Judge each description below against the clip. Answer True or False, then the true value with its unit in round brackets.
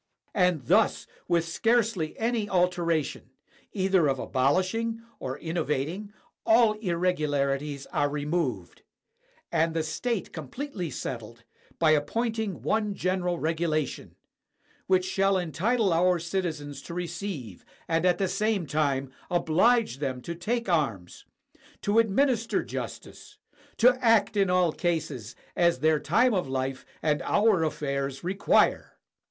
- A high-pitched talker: False (175 Hz)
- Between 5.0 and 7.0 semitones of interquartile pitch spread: True (5.4 semitones)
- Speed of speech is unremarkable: False (125 wpm)